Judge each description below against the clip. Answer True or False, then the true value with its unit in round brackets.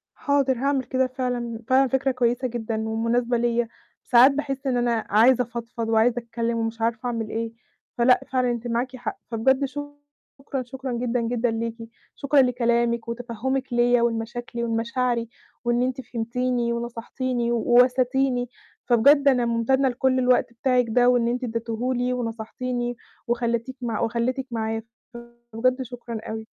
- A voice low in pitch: False (240 Hz)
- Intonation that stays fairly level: True (1.7 semitones)